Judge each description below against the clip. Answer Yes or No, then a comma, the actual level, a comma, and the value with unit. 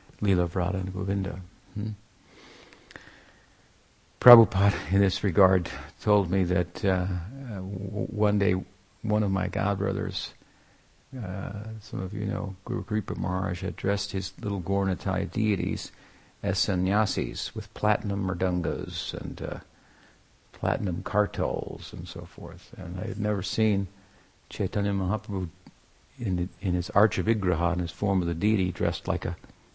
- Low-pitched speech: Yes, very low, 95 Hz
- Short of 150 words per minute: Yes, slow, 135 wpm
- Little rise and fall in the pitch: Yes, narrow, 2.2 semitones